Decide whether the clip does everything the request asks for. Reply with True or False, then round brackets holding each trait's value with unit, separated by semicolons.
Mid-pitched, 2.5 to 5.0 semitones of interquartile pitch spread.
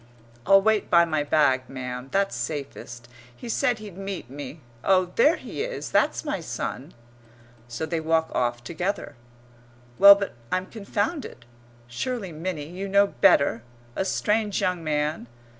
False (175 Hz; 5.5 semitones)